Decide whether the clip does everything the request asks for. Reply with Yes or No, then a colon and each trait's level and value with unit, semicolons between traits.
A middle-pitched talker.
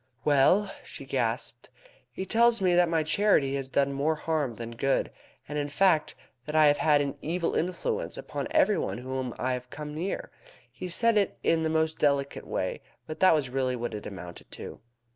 Yes: medium, 150 Hz